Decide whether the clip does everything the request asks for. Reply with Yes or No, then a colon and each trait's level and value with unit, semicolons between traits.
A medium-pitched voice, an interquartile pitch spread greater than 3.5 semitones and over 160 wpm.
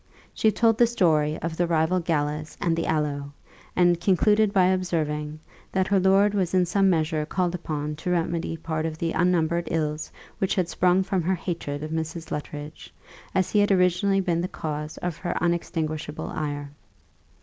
No: medium, 170 Hz; average, 3.0 semitones; average, 175 wpm